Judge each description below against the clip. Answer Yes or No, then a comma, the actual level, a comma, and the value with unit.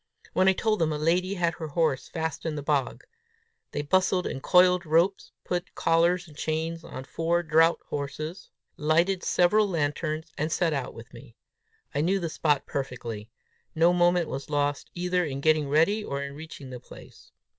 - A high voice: No, medium, 160 Hz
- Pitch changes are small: No, average, 3.4 semitones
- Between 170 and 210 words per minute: Yes, average, 175 wpm